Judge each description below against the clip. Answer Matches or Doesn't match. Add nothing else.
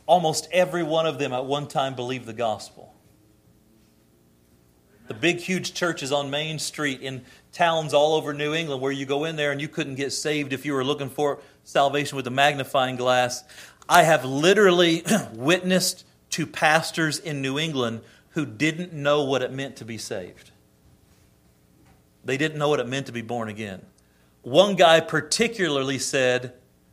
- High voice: Doesn't match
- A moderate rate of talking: Matches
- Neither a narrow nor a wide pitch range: Matches